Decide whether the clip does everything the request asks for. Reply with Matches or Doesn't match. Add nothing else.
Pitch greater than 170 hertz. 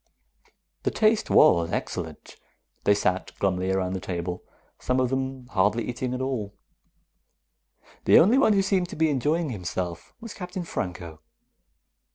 Doesn't match